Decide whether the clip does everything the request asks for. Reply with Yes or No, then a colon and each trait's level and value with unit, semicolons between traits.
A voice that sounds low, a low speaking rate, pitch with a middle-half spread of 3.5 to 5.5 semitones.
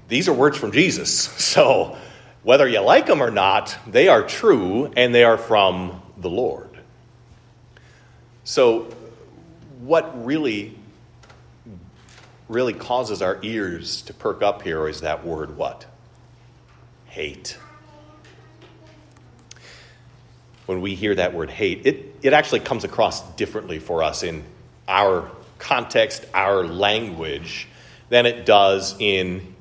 Yes: low, 115 Hz; slow, 120 wpm; average, 3.9 semitones